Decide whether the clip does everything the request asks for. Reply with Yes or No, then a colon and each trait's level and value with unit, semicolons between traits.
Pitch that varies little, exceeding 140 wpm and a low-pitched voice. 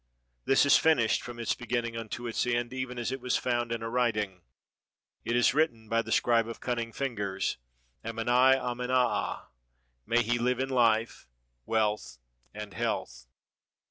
Yes: narrow, 1.7 semitones; average, 155 wpm; low, 120 Hz